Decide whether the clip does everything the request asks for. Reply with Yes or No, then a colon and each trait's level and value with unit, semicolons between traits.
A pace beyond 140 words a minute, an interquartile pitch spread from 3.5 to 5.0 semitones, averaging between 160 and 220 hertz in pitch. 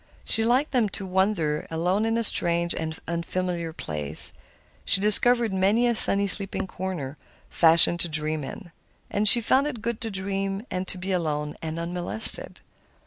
Yes: average, 160 wpm; average, 4.2 semitones; high, 190 Hz